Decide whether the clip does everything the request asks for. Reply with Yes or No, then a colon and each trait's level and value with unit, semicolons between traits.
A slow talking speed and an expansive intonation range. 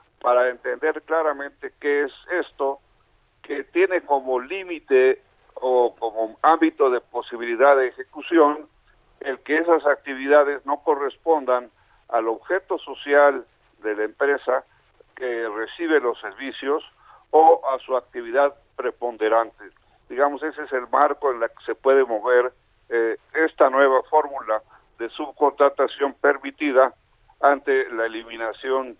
No: slow, 120 wpm; average, 4.5 semitones